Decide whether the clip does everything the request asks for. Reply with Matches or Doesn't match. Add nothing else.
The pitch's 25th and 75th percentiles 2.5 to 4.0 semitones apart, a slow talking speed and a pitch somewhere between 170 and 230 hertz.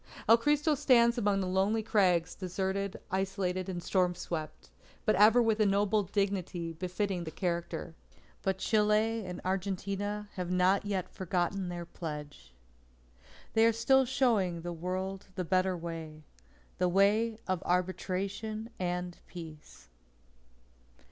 Matches